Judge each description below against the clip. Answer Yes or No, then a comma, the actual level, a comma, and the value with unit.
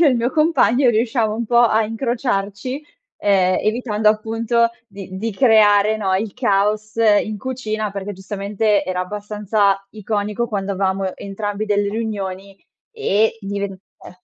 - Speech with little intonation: Yes, narrow, 2.1 semitones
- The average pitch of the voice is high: Yes, high, 210 Hz